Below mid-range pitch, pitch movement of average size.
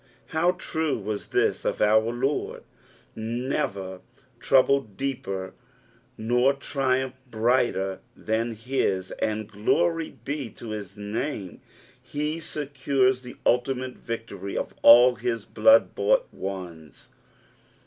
Yes: low, 120 Hz; average, 4.6 semitones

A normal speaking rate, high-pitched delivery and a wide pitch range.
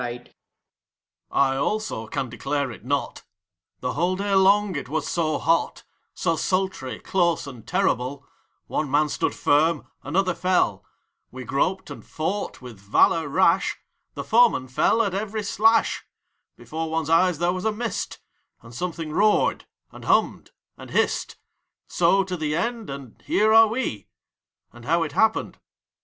No: average, 155 wpm; medium, 165 Hz; wide, 5.8 semitones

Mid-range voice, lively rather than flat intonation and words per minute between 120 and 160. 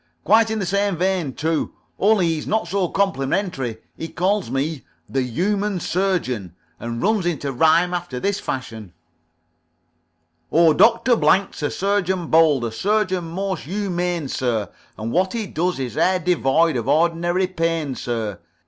Yes: medium, 170 Hz; wide, 6.0 semitones; average, 150 wpm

